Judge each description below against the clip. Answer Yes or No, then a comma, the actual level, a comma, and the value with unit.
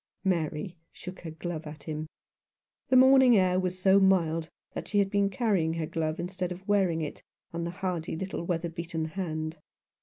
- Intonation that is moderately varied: Yes, average, 3.0 semitones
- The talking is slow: No, average, 180 wpm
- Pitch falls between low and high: Yes, medium, 175 Hz